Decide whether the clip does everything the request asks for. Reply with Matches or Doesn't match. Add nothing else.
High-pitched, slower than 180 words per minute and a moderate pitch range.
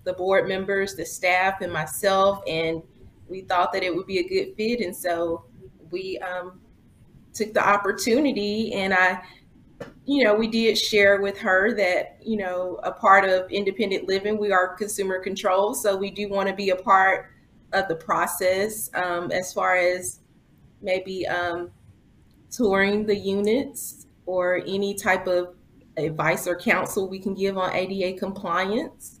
Doesn't match